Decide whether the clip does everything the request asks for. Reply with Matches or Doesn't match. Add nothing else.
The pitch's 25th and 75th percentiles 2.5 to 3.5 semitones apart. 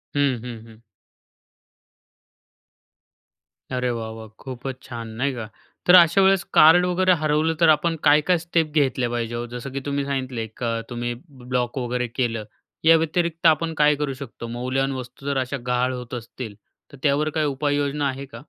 Doesn't match